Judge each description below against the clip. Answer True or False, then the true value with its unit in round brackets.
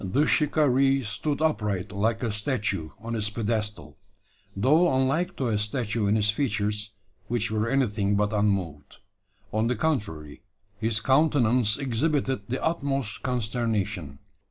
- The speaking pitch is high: False (110 Hz)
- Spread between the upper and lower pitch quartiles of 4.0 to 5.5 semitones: True (4.3 semitones)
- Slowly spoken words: True (130 wpm)